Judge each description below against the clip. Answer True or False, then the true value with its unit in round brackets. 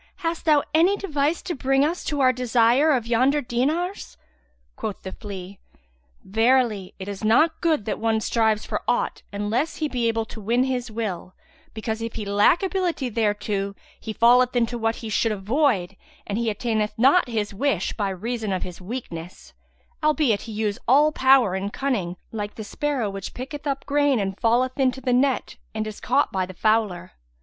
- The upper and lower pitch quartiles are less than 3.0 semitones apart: False (4.6 semitones)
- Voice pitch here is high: True (230 Hz)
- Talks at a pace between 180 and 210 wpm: True (185 wpm)